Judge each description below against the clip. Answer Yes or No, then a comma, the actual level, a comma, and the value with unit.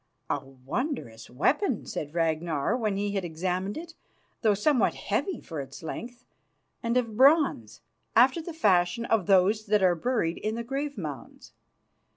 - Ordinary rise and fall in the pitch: No, wide, 7.1 semitones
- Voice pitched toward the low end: No, high, 205 Hz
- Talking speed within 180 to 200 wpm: No, average, 155 wpm